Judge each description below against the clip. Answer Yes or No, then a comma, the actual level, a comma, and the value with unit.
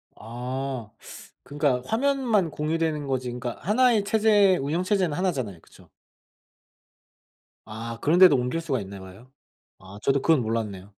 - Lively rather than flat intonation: Yes, wide, 7.7 semitones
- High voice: No, medium, 140 Hz